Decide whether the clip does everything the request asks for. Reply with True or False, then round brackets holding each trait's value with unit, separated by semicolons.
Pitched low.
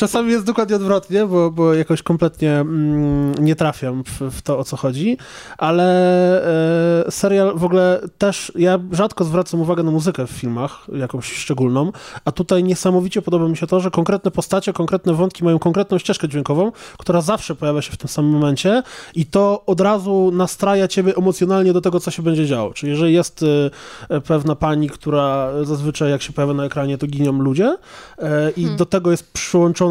False (170 Hz)